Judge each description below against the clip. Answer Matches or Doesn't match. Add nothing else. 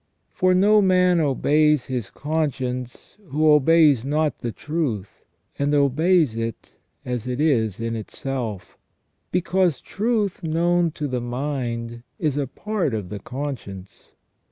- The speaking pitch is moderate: Matches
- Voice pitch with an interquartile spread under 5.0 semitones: Doesn't match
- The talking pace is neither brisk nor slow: Doesn't match